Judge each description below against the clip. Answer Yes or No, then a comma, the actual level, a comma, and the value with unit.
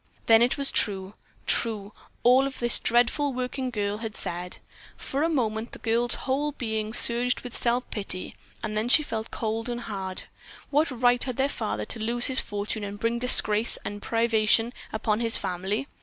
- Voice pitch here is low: No, high, 230 Hz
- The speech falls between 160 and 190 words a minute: Yes, average, 175 wpm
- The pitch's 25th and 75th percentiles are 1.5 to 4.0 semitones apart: Yes, average, 2.7 semitones